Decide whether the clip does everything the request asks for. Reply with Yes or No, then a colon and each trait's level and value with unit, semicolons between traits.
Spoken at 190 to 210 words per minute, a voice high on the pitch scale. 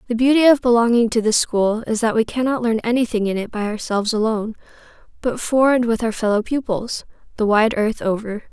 Yes: fast, 205 wpm; high, 230 Hz